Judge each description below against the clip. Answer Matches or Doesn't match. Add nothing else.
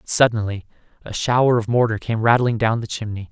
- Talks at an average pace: Matches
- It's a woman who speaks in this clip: Doesn't match